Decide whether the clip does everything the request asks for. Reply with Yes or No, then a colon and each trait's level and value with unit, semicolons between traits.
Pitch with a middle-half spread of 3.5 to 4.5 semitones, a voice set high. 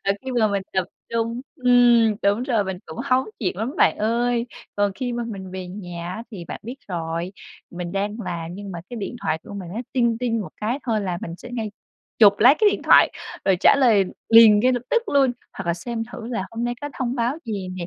Yes: average, 4.1 semitones; high, 220 Hz